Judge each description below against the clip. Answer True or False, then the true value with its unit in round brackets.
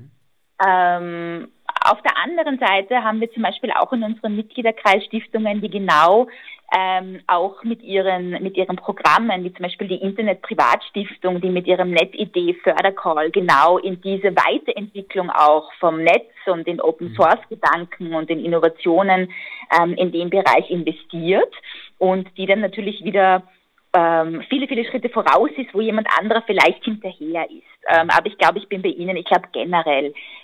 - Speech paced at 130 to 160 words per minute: True (155 wpm)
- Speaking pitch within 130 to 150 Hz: False (185 Hz)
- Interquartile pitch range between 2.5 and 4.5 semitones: True (3.7 semitones)